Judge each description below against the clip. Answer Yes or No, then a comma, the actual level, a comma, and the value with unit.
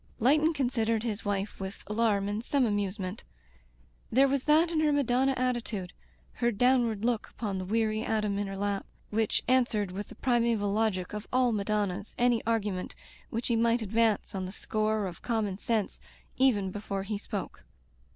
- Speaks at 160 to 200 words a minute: Yes, average, 170 wpm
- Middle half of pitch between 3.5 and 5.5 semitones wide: No, average, 3.1 semitones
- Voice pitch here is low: No, high, 220 Hz